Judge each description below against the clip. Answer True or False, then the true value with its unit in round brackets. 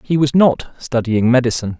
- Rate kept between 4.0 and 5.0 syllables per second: False (5.5 syllables/s)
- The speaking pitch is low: True (125 Hz)